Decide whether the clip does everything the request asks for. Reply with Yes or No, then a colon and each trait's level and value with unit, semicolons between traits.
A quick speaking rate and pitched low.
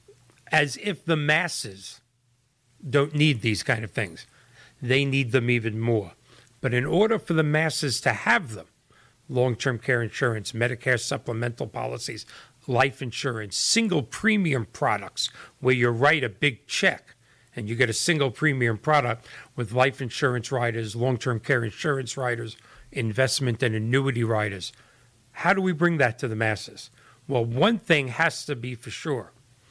No: average, 160 wpm; low, 125 Hz